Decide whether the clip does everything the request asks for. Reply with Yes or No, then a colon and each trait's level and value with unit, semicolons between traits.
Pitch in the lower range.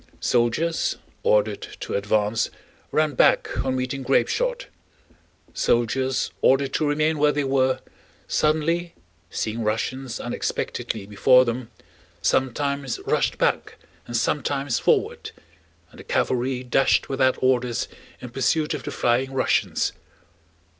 Yes: low, 130 Hz